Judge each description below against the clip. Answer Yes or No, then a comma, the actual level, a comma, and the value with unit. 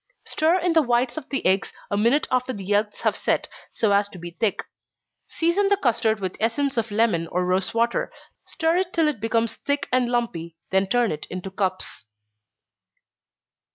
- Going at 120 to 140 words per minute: No, average, 180 wpm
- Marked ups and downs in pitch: Yes, wide, 6.0 semitones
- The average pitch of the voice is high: Yes, high, 230 Hz